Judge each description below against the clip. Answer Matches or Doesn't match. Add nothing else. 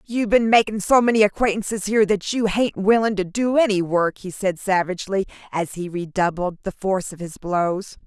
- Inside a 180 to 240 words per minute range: Matches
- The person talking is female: Matches